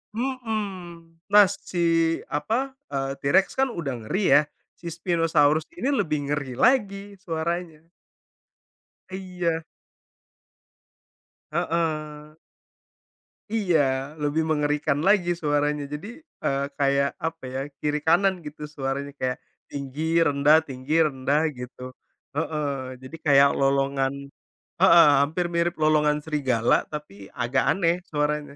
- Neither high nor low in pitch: Yes, medium, 150 Hz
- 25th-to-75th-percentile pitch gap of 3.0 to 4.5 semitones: Yes, average, 3.5 semitones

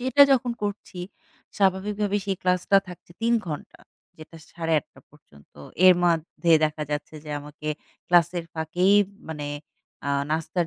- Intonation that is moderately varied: Yes, average, 4.1 semitones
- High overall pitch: No, medium, 175 Hz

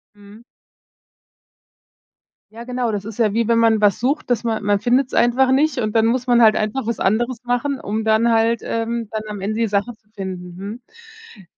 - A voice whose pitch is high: Yes, high, 225 Hz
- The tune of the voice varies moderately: No, narrow, 2.3 semitones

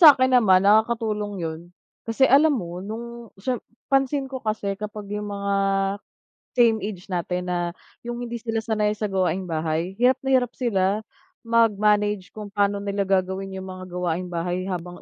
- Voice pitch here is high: Yes, high, 205 Hz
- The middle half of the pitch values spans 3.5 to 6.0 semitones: Yes, average, 3.9 semitones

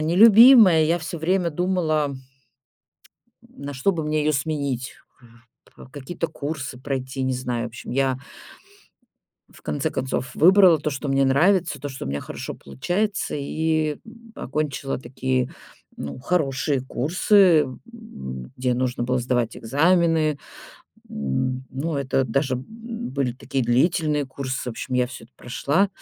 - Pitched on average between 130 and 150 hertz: Yes, medium, 140 Hz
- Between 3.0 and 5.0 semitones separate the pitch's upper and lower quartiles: Yes, average, 4.1 semitones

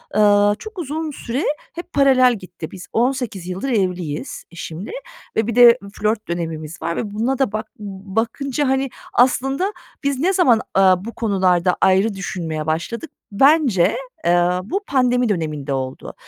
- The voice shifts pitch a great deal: Yes, wide, 6.5 semitones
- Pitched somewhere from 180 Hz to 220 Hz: Yes, high, 215 Hz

